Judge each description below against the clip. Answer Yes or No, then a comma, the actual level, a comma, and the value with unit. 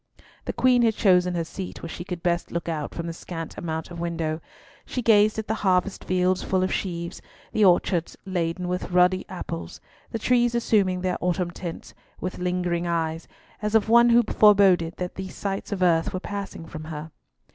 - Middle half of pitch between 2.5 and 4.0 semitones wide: Yes, average, 2.8 semitones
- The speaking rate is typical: Yes, average, 190 wpm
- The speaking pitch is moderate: Yes, medium, 180 Hz